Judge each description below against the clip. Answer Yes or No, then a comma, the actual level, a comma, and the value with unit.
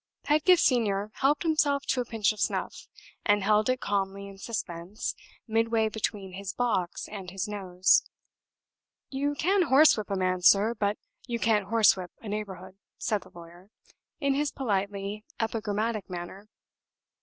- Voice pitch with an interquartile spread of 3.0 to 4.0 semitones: Yes, average, 3.3 semitones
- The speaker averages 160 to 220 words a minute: No, average, 145 wpm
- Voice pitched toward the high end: Yes, high, 210 Hz